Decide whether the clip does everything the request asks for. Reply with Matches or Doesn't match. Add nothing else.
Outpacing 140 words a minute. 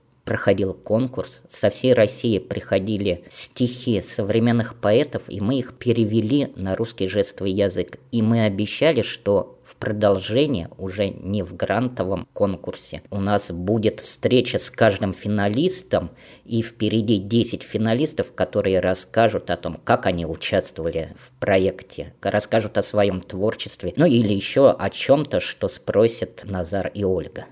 Doesn't match